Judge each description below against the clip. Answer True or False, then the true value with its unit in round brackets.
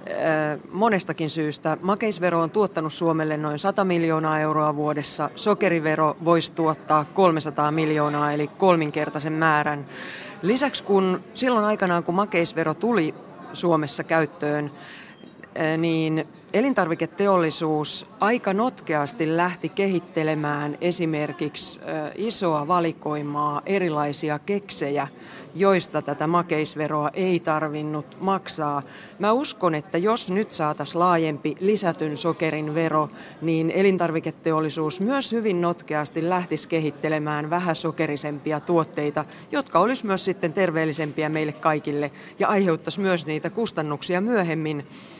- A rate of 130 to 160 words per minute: False (100 wpm)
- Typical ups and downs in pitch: True (3.1 semitones)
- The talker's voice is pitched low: False (160 Hz)